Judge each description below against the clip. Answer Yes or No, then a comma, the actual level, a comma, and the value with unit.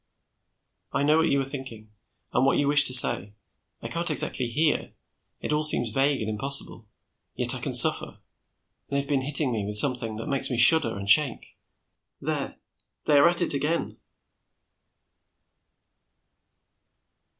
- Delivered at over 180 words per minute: No, average, 155 wpm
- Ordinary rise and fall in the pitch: Yes, average, 4.5 semitones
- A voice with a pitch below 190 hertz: Yes, low, 135 Hz